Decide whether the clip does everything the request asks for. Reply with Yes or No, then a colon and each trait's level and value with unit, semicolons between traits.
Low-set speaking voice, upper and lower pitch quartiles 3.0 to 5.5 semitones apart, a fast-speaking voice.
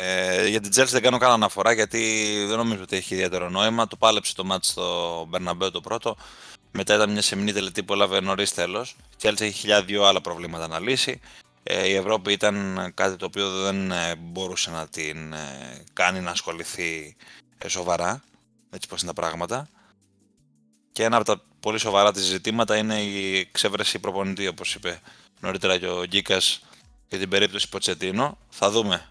No: low, 100 Hz; narrow, 2.6 semitones; fast, 175 wpm